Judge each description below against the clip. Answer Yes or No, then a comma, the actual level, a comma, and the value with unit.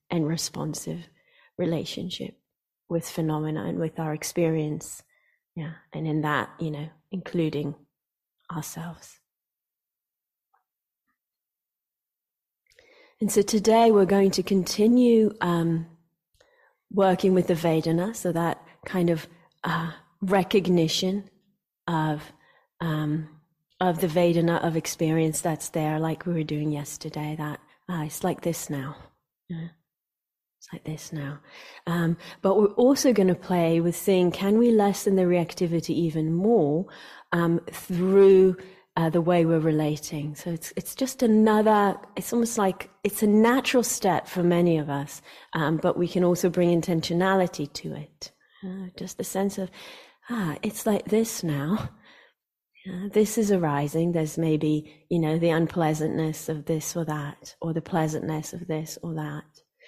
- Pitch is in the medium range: Yes, medium, 170 Hz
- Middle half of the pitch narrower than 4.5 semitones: Yes, average, 3.7 semitones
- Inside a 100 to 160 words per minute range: Yes, average, 140 wpm